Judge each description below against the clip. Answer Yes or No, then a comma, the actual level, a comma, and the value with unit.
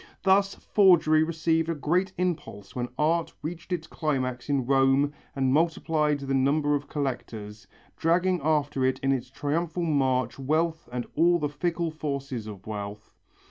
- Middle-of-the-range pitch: Yes, medium, 145 Hz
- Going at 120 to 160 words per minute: Yes, average, 150 wpm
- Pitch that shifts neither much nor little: Yes, average, 3.9 semitones